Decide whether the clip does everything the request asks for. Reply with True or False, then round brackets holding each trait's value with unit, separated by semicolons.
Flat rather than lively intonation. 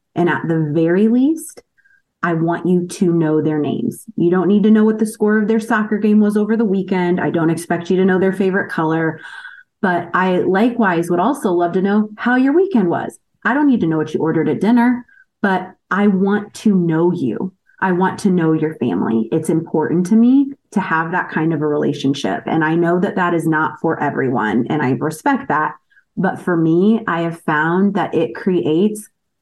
False (4.6 semitones)